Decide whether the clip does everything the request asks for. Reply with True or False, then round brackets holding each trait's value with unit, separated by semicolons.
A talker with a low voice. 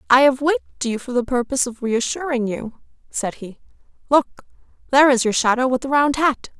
False (255 Hz)